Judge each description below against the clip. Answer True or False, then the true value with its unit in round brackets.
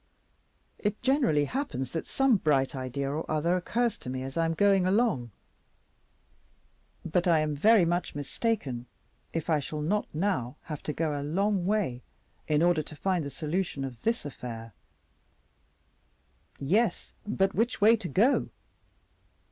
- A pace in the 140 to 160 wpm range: True (150 wpm)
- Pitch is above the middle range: False (165 Hz)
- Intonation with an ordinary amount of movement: False (6.2 semitones)